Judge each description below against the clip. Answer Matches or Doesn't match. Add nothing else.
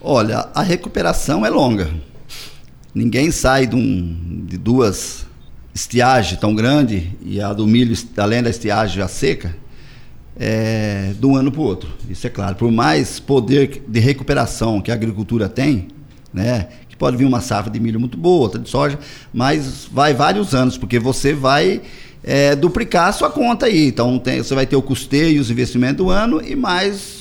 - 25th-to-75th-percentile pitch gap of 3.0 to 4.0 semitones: Doesn't match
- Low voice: Matches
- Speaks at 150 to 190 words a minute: Matches